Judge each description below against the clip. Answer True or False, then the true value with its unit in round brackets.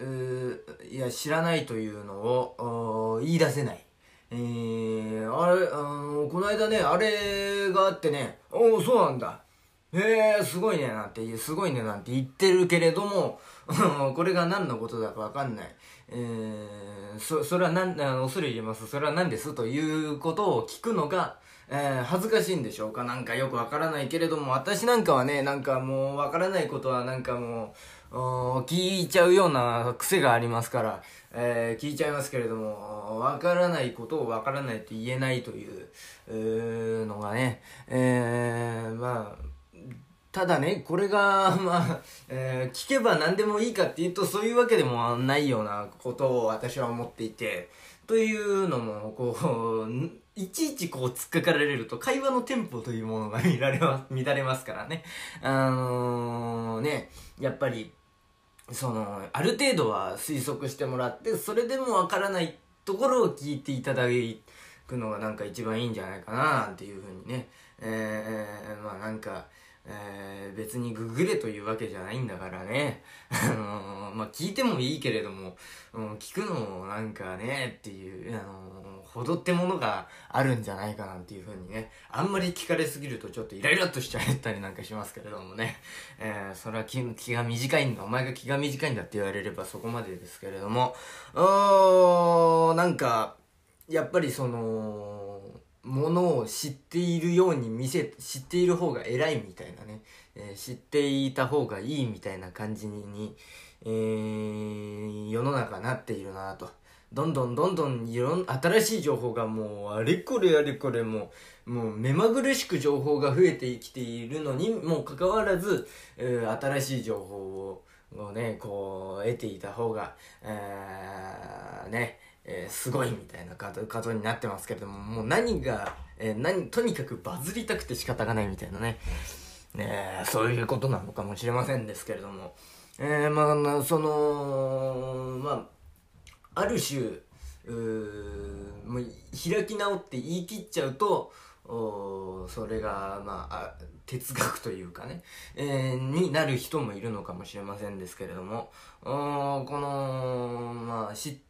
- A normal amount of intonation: False (6.1 semitones)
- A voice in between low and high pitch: False (125 Hz)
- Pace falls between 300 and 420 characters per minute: True (320 characters per minute)